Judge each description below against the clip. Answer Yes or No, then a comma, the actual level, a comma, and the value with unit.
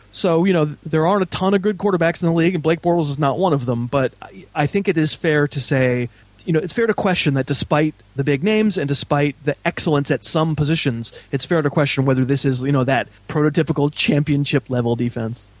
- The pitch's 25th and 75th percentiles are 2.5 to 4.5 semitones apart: Yes, average, 3.6 semitones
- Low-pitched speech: No, medium, 145 Hz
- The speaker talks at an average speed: No, fast, 235 wpm